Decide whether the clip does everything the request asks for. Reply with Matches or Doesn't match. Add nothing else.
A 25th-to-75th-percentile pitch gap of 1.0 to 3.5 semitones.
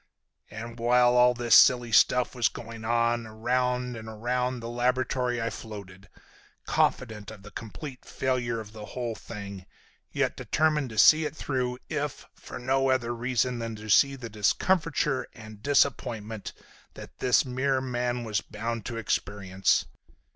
Matches